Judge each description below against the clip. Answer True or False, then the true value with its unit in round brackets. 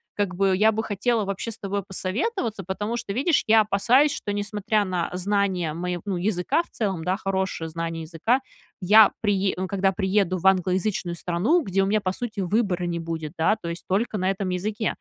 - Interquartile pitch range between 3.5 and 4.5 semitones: False (2.9 semitones)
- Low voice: False (195 Hz)